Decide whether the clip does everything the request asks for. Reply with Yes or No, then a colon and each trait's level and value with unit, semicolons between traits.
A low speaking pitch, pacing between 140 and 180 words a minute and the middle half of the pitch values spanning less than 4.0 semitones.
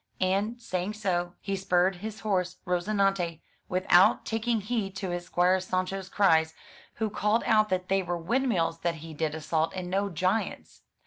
No: medium, 185 Hz; average, 170 wpm; average, 2.8 semitones